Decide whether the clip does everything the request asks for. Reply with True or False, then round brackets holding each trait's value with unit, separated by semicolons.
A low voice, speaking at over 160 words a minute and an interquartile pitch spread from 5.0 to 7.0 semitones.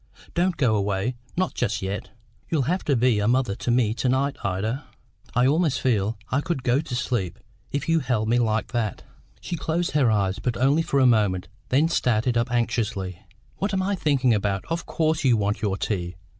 True (125 Hz; 200 wpm; 5.4 semitones)